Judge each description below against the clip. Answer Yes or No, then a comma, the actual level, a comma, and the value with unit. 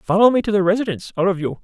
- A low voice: No, high, 195 Hz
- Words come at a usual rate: No, fast, 255 wpm